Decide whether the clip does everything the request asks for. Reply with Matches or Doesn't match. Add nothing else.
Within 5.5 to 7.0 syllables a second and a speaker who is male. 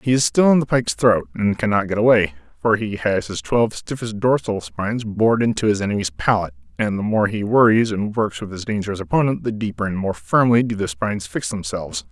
Matches